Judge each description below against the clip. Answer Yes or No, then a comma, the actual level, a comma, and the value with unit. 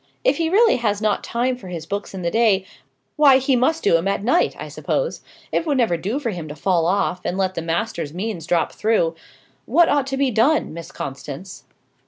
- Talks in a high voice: Yes, high, 210 Hz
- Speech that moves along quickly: Yes, fast, 220 wpm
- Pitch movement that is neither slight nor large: No, wide, 7.1 semitones